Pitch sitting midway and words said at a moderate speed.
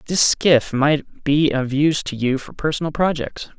Yes: medium, 145 Hz; average, 185 wpm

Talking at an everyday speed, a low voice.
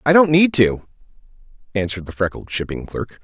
Yes: average, 165 wpm; low, 125 Hz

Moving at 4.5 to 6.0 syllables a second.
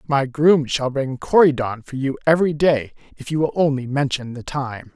Yes: 5.0 syllables/s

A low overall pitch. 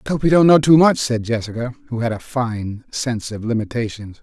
Yes: low, 120 Hz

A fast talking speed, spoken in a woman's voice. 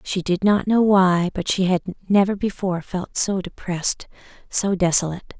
No: average, 165 wpm; female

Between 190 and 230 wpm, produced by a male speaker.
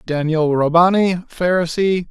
No: slow, 85 wpm; male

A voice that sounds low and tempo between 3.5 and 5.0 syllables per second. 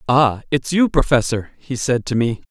Yes: low, 130 Hz; 4.7 syllables/s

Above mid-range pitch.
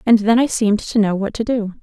Yes: high, 215 Hz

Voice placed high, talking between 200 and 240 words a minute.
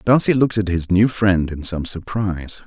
No: very low, 95 Hz; fast, 205 wpm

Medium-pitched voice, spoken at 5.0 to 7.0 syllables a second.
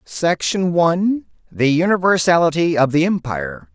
No: medium, 160 Hz; 4.7 syllables/s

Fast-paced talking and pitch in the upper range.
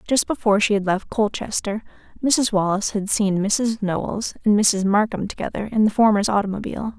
No: average, 170 wpm; high, 210 Hz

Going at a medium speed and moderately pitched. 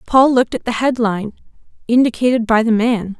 No: average, 170 wpm; high, 235 Hz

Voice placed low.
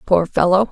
No: high, 190 Hz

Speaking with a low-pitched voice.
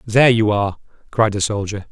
Yes: low, 105 Hz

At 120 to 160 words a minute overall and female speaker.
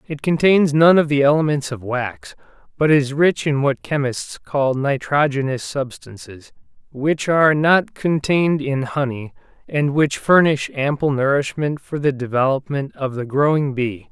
No: average, 150 wpm; male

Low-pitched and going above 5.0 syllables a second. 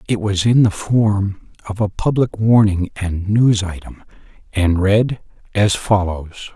No: low, 100 Hz; 3.8 syllables/s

